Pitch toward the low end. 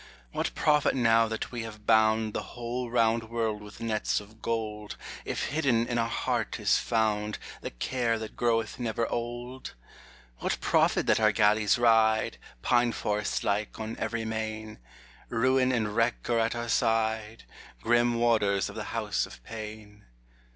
Yes: low, 115 Hz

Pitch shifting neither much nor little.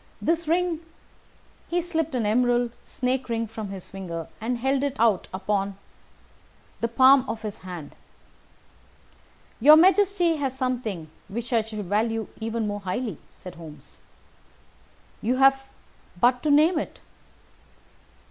Yes: average, 4.8 semitones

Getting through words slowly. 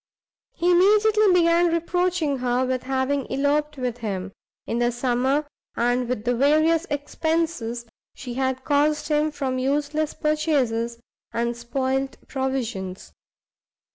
Yes: slow, 120 wpm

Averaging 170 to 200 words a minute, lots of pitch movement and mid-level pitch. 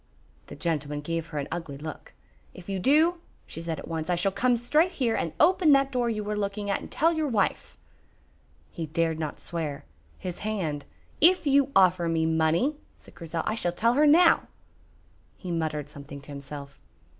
Yes: average, 190 wpm; wide, 7.5 semitones; medium, 175 Hz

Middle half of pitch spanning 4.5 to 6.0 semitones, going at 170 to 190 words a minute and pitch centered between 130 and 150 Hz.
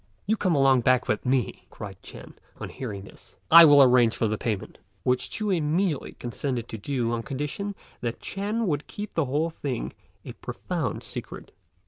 Yes: wide, 5.6 semitones; average, 175 wpm; low, 135 Hz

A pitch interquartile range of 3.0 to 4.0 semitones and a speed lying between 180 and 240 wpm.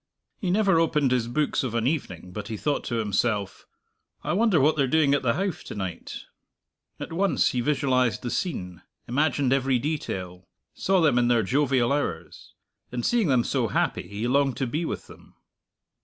No: average, 4.8 semitones; average, 185 wpm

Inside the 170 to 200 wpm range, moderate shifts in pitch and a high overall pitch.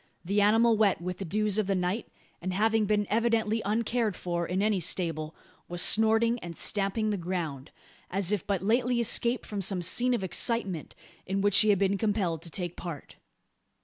Yes: average, 185 wpm; average, 3.5 semitones; high, 200 Hz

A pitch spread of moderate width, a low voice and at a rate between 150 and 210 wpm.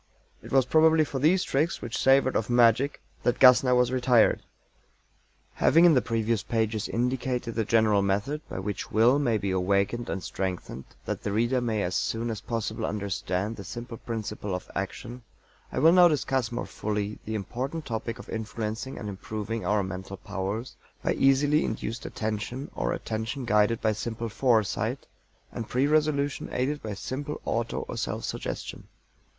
Yes: average, 3.6 semitones; low, 115 Hz; average, 165 wpm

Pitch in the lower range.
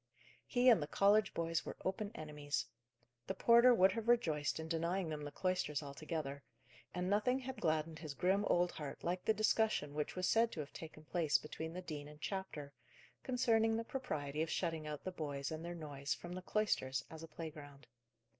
No: medium, 165 Hz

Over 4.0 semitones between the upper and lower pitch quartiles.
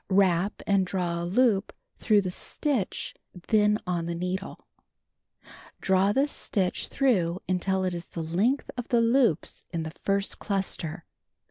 No: average, 3.1 semitones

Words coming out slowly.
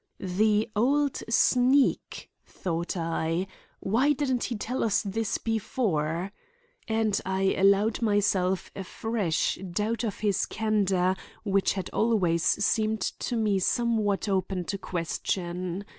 Yes: slow, 120 wpm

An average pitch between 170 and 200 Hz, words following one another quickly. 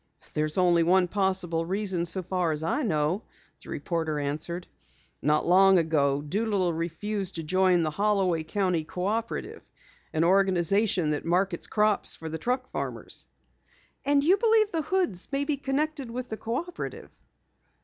No: medium, 185 Hz; average, 150 wpm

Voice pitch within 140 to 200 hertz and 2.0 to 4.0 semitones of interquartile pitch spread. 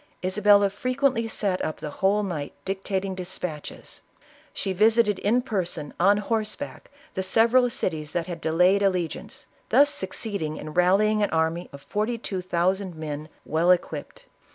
Yes: high, 190 Hz; average, 3.7 semitones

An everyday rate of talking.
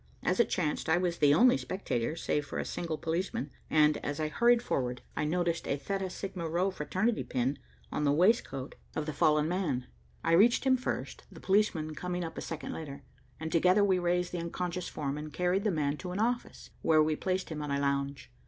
No: fast, 210 wpm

